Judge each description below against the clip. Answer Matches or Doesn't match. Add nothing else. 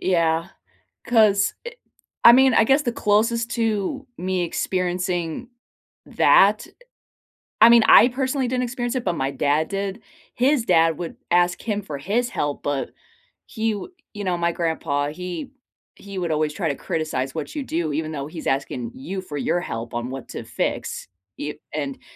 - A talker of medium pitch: Matches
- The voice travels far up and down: Matches